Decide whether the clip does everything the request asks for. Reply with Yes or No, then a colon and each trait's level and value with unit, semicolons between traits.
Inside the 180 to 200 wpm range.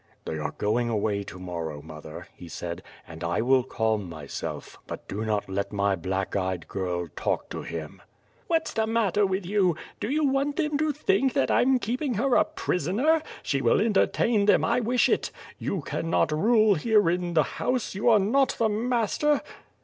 Yes: average, 190 wpm